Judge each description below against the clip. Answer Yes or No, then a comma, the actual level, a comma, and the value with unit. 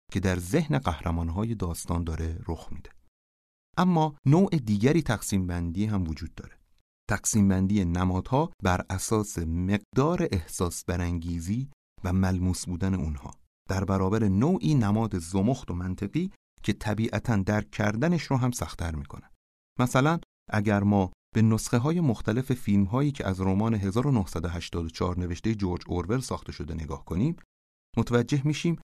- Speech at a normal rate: Yes, average, 135 wpm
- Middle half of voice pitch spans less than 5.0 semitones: No, wide, 5.5 semitones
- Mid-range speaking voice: No, very low, 95 Hz